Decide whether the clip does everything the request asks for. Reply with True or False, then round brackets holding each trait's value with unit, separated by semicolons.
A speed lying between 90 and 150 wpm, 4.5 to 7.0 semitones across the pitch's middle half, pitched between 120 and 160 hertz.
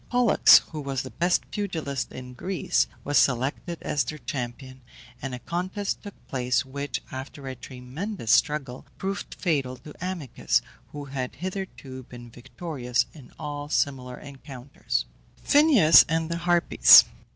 True (140 wpm; 5.1 semitones; 140 Hz)